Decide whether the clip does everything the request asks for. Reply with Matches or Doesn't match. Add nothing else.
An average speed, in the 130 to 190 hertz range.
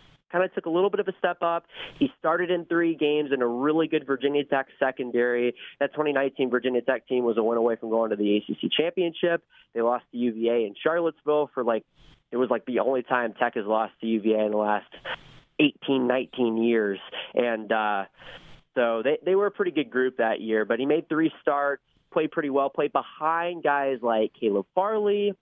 Doesn't match